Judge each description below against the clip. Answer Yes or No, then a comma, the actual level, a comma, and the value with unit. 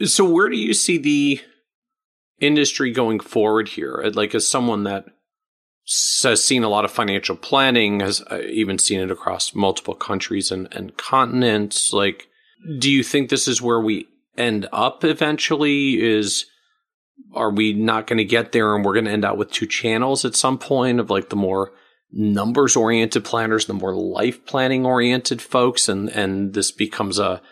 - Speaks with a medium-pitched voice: No, low, 120 Hz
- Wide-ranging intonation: No, average, 4.8 semitones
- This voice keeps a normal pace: Yes, average, 175 wpm